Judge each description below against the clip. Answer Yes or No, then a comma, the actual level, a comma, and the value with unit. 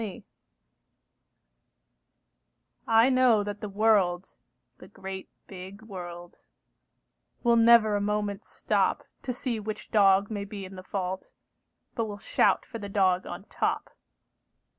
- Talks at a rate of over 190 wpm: No, average, 140 wpm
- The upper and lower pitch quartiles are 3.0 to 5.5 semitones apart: No, narrow, 2.5 semitones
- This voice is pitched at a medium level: No, high, 205 Hz